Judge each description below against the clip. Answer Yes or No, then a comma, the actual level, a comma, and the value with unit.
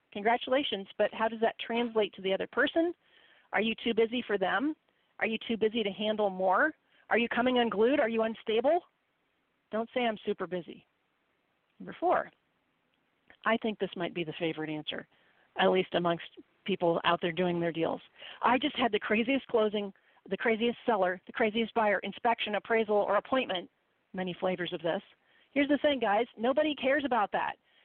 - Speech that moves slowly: No, average, 175 wpm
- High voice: Yes, high, 220 Hz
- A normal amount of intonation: Yes, average, 4.0 semitones